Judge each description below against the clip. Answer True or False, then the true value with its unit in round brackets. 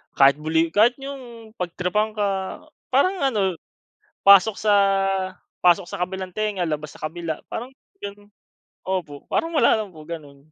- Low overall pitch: False (190 Hz)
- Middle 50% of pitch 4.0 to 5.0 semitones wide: True (4.6 semitones)